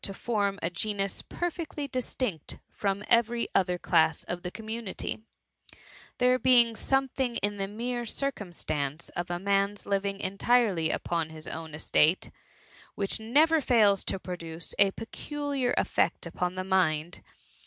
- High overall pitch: Yes, high, 200 Hz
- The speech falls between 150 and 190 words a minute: No, average, 140 wpm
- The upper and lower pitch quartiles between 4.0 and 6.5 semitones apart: Yes, average, 5.2 semitones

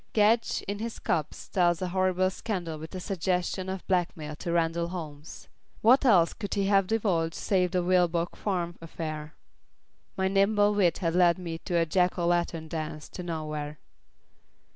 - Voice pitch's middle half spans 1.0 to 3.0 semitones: Yes, narrow, 2.6 semitones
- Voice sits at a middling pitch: Yes, medium, 175 Hz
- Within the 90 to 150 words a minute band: No, average, 165 wpm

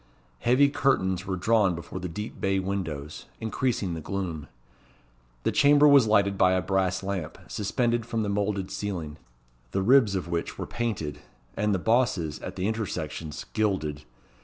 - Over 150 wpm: Yes, average, 160 wpm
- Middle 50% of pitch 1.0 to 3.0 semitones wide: No, average, 4.0 semitones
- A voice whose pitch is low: Yes, very low, 95 Hz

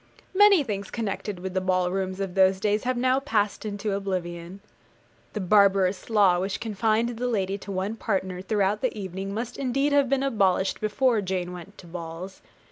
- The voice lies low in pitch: No, high, 200 Hz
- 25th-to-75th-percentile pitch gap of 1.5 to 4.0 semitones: Yes, average, 3.2 semitones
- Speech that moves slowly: No, average, 180 wpm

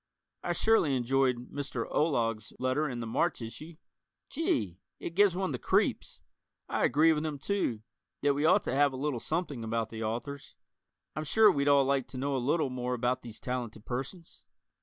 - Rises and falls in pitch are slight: No, average, 4.2 semitones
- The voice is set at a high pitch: No, low, 135 Hz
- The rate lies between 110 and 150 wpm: No, average, 185 wpm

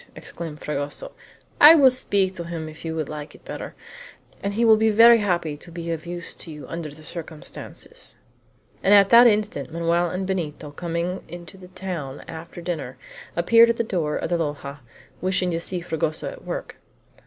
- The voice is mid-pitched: Yes, medium, 170 Hz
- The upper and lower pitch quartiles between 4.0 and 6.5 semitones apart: No, average, 3.6 semitones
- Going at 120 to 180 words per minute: No, average, 190 wpm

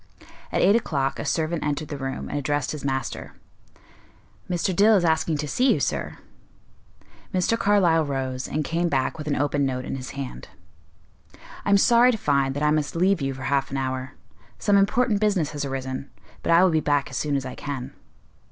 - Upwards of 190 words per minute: Yes, average, 200 wpm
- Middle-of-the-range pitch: Yes, medium, 150 Hz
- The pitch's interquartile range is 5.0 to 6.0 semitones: No, average, 4.6 semitones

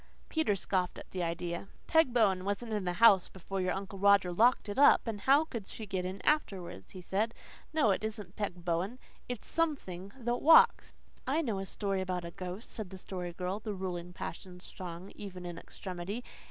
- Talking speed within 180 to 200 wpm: Yes, average, 195 wpm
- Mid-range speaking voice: No, high, 195 Hz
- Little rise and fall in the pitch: No, average, 3.5 semitones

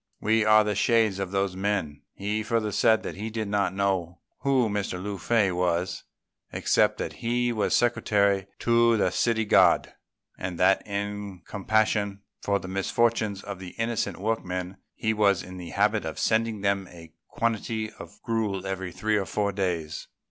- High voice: No, low, 100 Hz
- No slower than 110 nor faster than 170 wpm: Yes, average, 165 wpm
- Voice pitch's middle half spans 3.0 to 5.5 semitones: No, narrow, 2.6 semitones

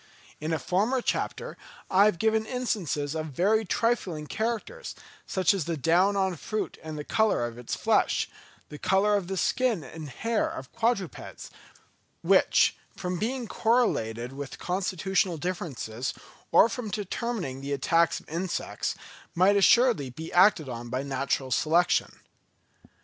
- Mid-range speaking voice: Yes, medium, 180 Hz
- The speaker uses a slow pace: No, average, 145 wpm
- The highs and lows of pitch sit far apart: Yes, wide, 6.7 semitones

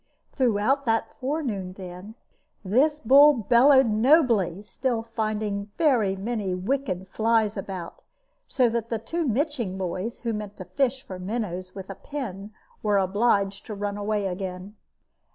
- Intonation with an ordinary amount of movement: Yes, average, 4.2 semitones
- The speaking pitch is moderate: No, high, 215 Hz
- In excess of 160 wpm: No, slow, 135 wpm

